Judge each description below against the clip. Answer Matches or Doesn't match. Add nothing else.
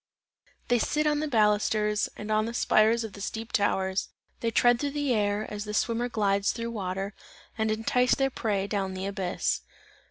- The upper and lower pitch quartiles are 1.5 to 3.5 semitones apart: Matches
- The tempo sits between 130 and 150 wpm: Doesn't match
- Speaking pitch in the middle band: Doesn't match